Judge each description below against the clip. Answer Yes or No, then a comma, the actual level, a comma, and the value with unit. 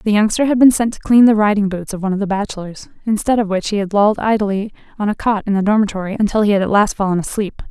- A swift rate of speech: Yes, fast, 270 wpm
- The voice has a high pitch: Yes, high, 205 Hz